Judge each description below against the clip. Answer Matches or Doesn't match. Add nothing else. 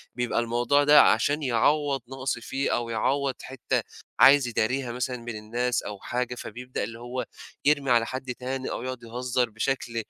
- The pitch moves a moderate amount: Doesn't match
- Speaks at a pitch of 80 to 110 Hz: Doesn't match